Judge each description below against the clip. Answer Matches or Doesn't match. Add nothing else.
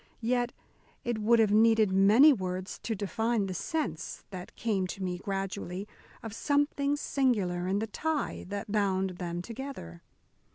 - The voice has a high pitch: Matches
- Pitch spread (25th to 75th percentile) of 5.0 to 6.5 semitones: Doesn't match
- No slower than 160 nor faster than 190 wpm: Doesn't match